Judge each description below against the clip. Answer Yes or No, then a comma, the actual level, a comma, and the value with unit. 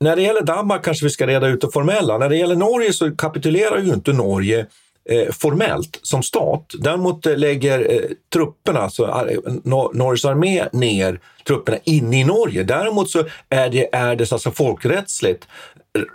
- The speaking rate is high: No, average, 155 wpm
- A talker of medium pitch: Yes, medium, 155 Hz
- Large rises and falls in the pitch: Yes, wide, 6.5 semitones